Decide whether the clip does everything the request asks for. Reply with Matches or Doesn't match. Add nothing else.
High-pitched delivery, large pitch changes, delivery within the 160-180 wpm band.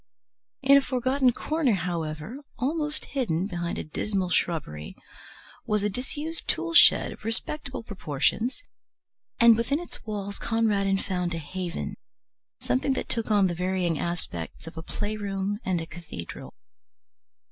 Doesn't match